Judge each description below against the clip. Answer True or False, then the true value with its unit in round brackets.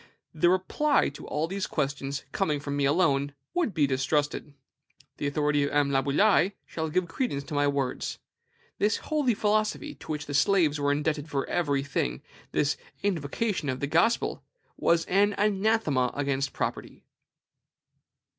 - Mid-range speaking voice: True (150 Hz)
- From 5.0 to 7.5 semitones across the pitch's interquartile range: True (5.4 semitones)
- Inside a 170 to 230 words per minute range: False (150 wpm)